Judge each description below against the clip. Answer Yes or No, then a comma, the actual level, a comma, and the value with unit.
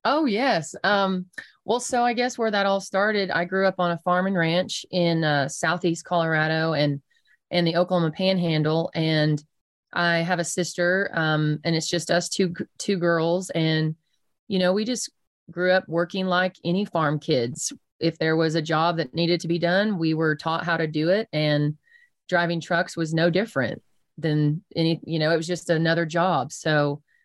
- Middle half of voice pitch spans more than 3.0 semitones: No, narrow, 2.4 semitones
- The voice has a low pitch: No, medium, 170 Hz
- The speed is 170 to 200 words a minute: Yes, average, 190 wpm